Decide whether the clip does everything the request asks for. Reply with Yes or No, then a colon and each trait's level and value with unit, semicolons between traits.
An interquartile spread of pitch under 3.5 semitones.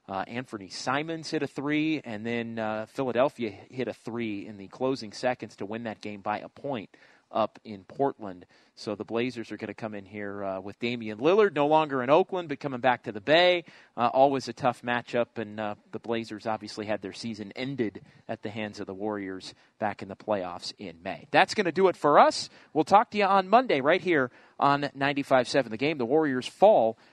No: average, 4.8 semitones